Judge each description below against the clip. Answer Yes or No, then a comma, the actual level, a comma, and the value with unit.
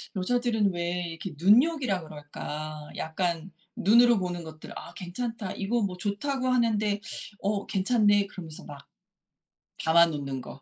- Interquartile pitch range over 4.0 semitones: Yes, average, 5.2 semitones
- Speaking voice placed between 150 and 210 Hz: Yes, high, 190 Hz